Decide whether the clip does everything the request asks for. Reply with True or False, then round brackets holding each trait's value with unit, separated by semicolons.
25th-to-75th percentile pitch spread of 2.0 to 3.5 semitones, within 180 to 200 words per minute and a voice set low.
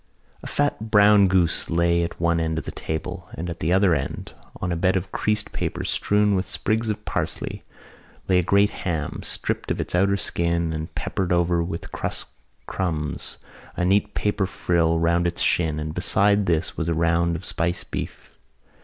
True (2.8 semitones; 185 wpm; 85 Hz)